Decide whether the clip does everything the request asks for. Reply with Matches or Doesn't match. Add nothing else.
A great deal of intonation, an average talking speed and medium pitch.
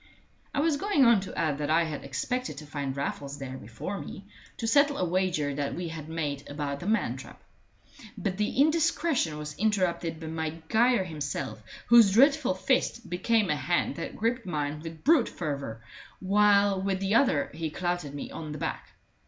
Matches